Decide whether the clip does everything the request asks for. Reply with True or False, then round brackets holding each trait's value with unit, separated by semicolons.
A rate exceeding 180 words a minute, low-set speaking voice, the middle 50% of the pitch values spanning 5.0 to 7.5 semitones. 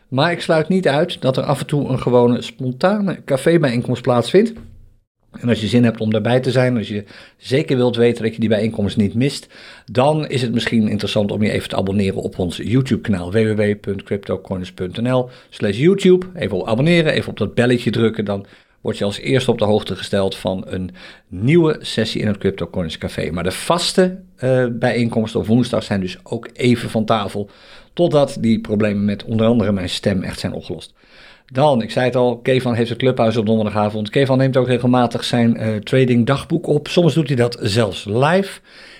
False (195 wpm; 120 Hz; 3.7 semitones)